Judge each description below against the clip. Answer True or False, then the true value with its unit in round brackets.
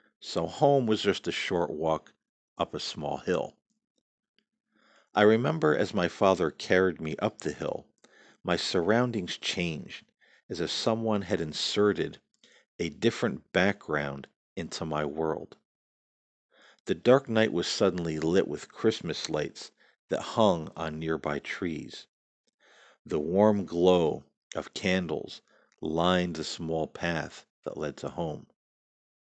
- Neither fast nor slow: False (125 wpm)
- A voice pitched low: True (95 Hz)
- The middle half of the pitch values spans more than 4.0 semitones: True (5.5 semitones)